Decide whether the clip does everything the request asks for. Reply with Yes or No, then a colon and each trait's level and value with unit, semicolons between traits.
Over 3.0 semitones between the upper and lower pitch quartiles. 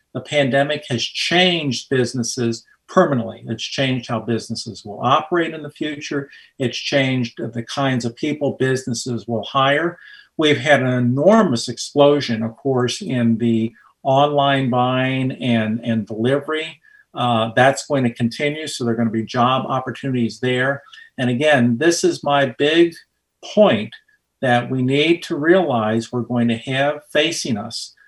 Yes: average, 3.6 semitones